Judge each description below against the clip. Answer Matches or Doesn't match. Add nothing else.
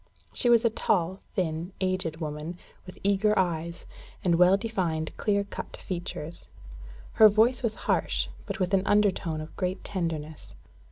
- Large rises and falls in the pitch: Doesn't match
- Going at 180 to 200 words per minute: Doesn't match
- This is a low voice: Doesn't match